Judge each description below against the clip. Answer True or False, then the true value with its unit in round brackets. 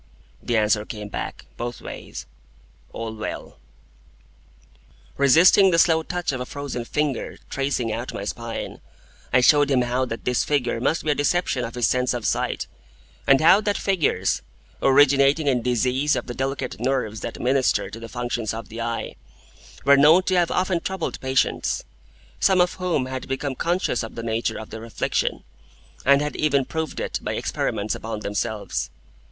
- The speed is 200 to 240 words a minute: False (170 wpm)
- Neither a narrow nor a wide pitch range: True (4.3 semitones)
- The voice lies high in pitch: False (130 Hz)